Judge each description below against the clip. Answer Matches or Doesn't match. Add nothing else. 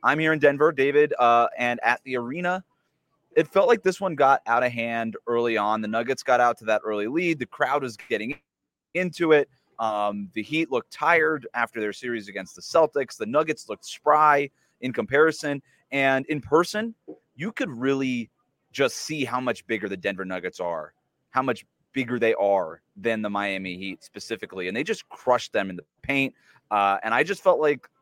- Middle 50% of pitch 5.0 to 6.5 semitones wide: Matches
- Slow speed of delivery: Doesn't match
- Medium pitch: Doesn't match